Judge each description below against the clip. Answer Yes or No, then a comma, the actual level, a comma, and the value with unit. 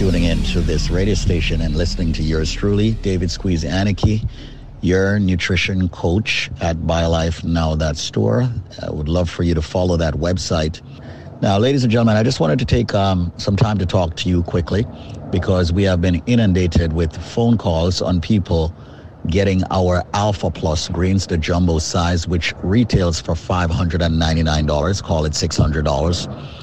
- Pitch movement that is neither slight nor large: Yes, average, 3.1 semitones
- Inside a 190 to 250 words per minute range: No, average, 165 wpm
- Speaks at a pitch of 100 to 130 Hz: No, very low, 90 Hz